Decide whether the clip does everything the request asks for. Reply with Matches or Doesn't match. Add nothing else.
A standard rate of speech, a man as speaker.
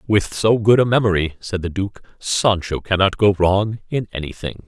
Matches